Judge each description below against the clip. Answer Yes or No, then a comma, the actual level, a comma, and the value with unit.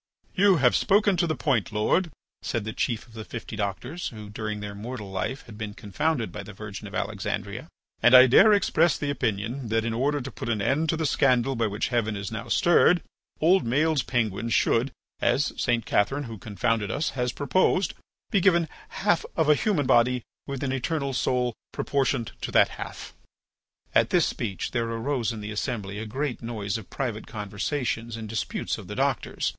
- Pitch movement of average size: Yes, average, 4.9 semitones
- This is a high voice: No, low, 120 Hz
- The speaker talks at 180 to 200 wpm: Yes, average, 195 wpm